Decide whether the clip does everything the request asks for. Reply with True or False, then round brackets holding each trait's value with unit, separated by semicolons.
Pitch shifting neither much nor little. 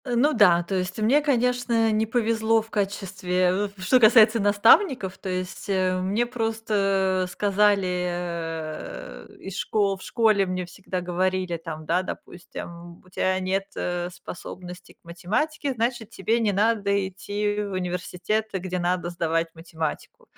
True (3.5 semitones)